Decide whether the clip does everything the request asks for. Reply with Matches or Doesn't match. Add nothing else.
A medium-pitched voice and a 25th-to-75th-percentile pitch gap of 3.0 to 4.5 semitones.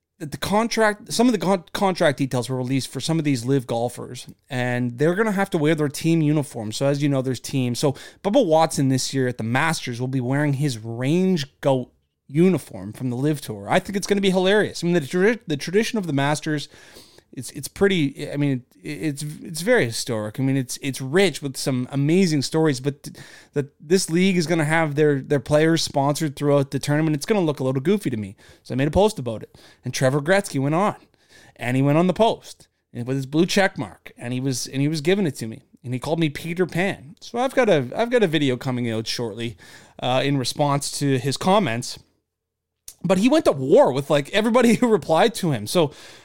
Doesn't match